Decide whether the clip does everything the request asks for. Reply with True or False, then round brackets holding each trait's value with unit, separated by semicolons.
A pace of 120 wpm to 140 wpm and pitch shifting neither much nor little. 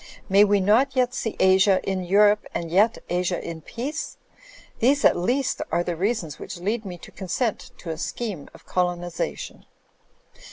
False (170 wpm; 4.6 semitones)